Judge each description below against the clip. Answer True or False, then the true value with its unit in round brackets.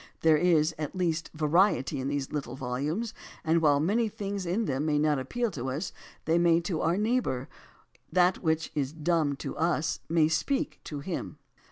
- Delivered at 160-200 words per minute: True (180 wpm)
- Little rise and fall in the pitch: False (3.5 semitones)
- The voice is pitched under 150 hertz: False (160 Hz)